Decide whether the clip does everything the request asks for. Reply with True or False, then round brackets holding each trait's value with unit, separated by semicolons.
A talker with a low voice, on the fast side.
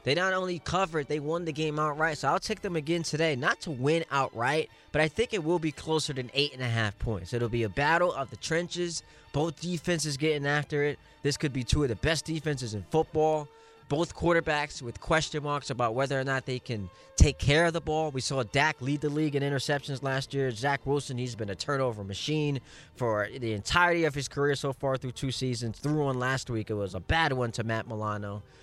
False (145 Hz; 230 wpm)